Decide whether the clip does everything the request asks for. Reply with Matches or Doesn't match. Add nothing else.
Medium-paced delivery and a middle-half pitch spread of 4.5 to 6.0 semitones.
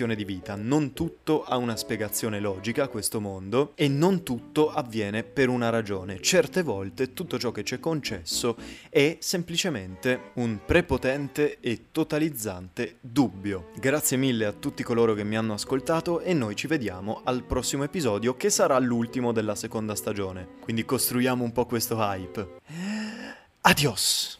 Matches